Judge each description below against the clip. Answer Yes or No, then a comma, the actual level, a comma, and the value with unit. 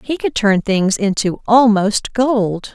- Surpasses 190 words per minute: No, average, 155 wpm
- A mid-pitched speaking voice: No, high, 215 Hz